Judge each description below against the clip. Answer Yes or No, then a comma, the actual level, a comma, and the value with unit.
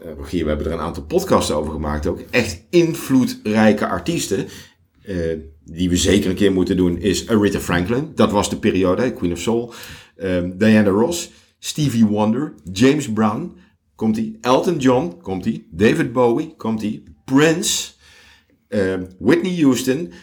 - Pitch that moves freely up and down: Yes, wide, 6.0 semitones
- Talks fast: No, average, 140 wpm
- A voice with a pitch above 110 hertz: No, low, 105 Hz